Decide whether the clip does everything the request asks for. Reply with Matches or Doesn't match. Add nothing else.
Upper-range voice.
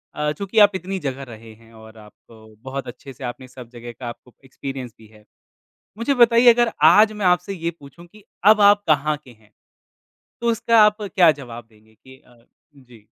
Doesn't match